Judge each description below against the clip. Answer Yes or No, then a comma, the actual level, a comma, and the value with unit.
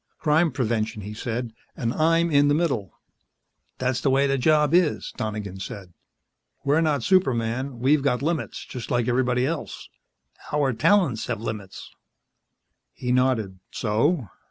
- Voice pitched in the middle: No, low, 130 Hz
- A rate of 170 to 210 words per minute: No, average, 140 wpm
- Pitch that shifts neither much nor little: Yes, average, 4.8 semitones